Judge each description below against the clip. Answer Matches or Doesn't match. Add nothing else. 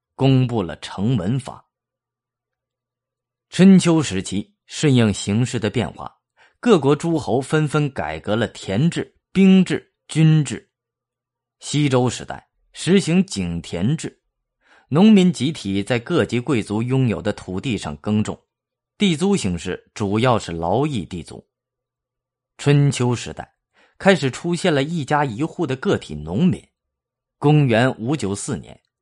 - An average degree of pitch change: Doesn't match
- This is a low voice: Matches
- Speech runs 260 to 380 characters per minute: Doesn't match